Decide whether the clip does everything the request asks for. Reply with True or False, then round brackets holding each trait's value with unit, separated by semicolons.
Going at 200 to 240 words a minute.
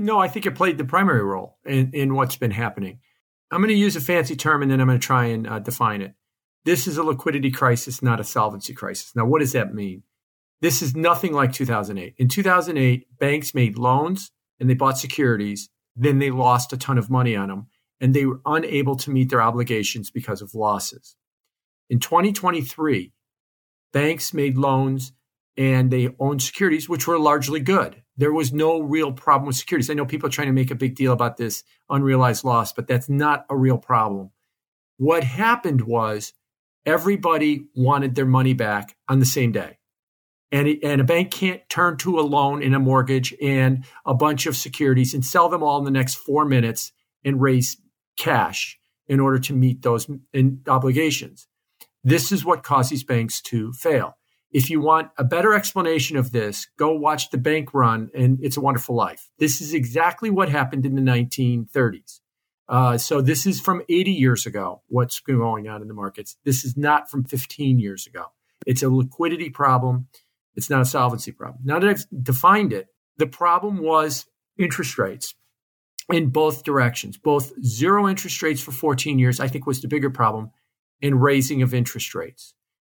False (190 wpm)